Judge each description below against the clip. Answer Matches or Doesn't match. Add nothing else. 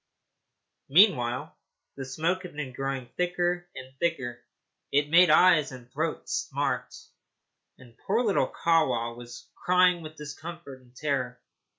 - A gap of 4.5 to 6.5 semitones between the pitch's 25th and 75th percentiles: Matches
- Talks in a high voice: Doesn't match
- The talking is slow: Matches